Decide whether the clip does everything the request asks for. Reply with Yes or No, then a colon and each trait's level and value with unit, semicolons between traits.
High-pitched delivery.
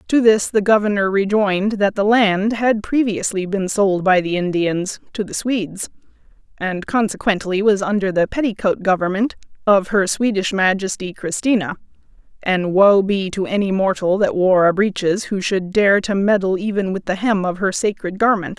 Yes: high, 200 Hz